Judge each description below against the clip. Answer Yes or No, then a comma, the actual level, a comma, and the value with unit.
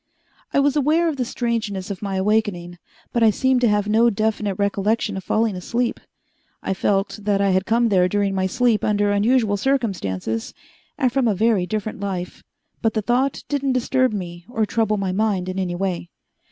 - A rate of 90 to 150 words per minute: No, average, 190 wpm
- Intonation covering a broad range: No, average, 3.6 semitones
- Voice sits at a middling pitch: No, high, 210 Hz